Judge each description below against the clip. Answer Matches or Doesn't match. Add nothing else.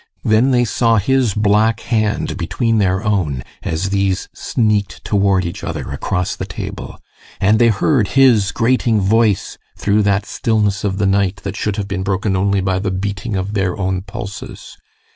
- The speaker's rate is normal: Matches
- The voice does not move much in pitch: Matches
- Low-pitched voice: Matches